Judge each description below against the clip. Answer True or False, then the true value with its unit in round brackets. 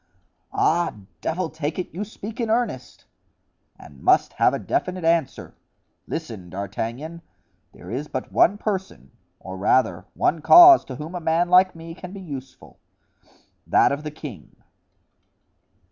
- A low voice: False (160 Hz)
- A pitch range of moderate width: False (6.0 semitones)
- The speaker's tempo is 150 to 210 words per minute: False (140 wpm)